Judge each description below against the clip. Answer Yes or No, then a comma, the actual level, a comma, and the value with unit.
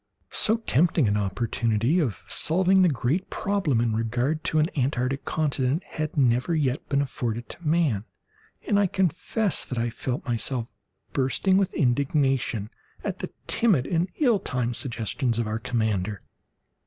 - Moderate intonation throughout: No, wide, 5.9 semitones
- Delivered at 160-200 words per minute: No, average, 150 wpm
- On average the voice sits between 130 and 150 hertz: Yes, low, 135 Hz